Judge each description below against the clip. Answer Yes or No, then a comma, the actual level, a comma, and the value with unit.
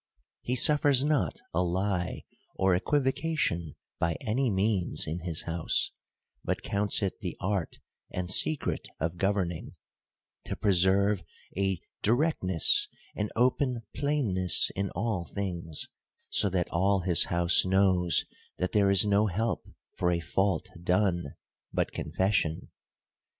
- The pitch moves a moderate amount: Yes, average, 3.3 semitones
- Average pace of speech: No, slow, 130 wpm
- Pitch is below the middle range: Yes, very low, 95 Hz